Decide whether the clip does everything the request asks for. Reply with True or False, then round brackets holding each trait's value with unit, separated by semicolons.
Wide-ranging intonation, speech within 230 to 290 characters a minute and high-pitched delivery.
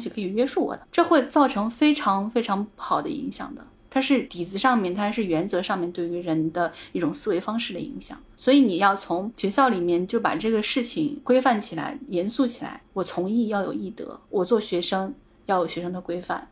False (6.5 semitones; 310 characters per minute; 205 Hz)